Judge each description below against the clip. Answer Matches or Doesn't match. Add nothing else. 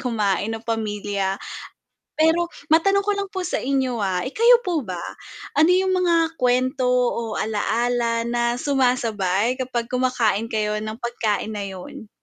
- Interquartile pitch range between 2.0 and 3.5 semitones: Doesn't match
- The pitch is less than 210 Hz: Doesn't match